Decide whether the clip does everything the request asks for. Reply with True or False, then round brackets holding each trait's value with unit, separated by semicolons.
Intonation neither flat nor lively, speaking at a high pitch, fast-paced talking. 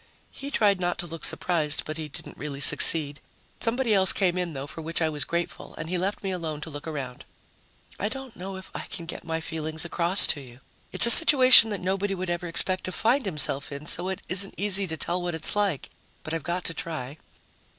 False (3.7 semitones; 175 Hz; 225 wpm)